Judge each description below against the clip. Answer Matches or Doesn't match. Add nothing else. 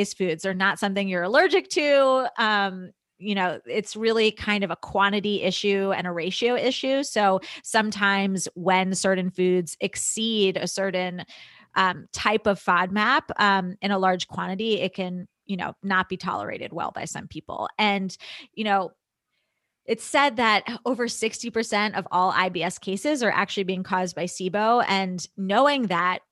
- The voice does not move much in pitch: Doesn't match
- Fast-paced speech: Doesn't match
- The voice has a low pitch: Doesn't match